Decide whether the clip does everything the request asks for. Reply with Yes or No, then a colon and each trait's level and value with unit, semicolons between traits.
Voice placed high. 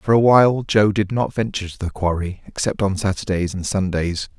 No: low, 100 Hz